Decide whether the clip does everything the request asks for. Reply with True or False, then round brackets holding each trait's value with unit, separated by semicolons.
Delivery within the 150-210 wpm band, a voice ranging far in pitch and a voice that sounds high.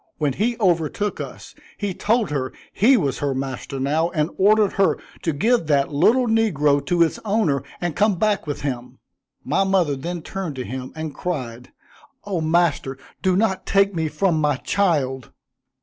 False (170 wpm; 5.8 semitones; 165 Hz)